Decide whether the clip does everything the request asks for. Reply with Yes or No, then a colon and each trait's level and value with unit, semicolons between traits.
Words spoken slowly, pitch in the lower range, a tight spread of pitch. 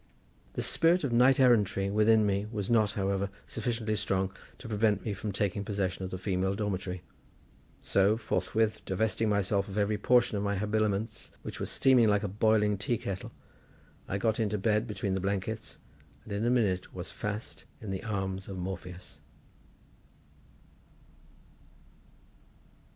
No: average, 150 wpm; low, 105 Hz; narrow, 2.2 semitones